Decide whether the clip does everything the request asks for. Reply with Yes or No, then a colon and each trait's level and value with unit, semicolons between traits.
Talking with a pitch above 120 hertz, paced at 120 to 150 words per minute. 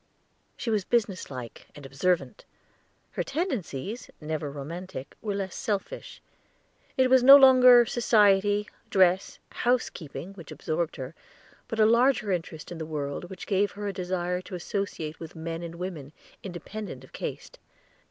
Yes: medium, 185 Hz; average, 145 wpm